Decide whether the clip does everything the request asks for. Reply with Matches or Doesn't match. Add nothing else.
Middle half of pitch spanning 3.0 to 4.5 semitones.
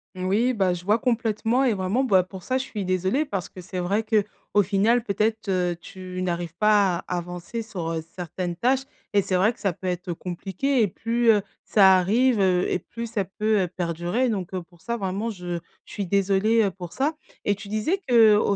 Matches